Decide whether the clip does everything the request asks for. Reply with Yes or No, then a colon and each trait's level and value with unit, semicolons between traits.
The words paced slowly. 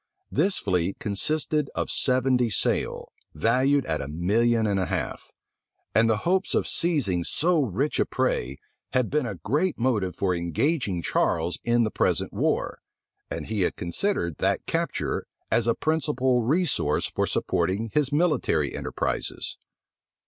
No: average, 145 wpm